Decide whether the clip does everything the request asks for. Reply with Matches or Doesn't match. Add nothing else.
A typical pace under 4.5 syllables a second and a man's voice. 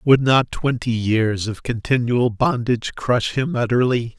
Matches